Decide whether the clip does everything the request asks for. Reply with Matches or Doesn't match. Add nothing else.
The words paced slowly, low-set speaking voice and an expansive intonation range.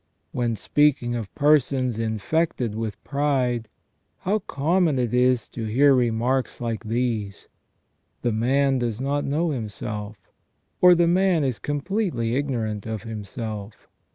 Doesn't match